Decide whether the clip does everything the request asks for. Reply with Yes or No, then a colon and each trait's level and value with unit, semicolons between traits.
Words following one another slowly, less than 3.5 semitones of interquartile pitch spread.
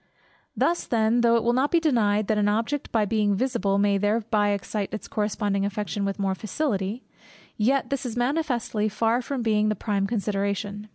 No: average, 180 wpm; average, 2.7 semitones